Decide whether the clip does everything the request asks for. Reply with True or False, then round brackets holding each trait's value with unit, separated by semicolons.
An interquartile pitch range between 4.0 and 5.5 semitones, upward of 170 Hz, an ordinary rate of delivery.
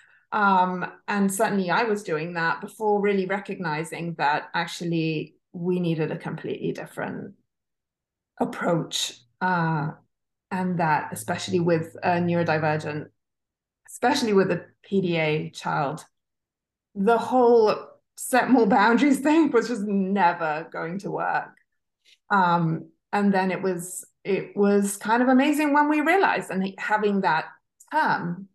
False (4.4 semitones; 190 Hz; 125 wpm)